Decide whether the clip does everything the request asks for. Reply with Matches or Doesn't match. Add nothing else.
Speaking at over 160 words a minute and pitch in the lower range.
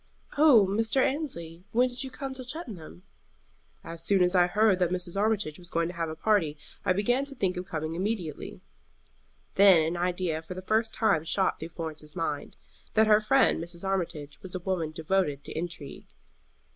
Doesn't match